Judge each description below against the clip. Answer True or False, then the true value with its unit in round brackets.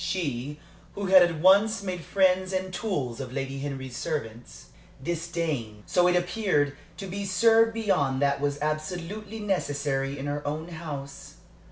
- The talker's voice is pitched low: False (165 Hz)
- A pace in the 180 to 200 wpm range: False (150 wpm)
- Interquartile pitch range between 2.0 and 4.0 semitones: False (5.1 semitones)